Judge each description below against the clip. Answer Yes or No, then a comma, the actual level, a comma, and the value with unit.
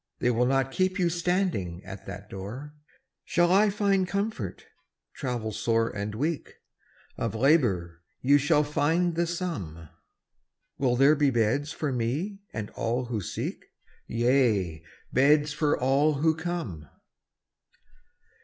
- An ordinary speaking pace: No, slow, 130 wpm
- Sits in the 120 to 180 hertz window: Yes, low, 135 Hz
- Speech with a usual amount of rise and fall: No, wide, 6.8 semitones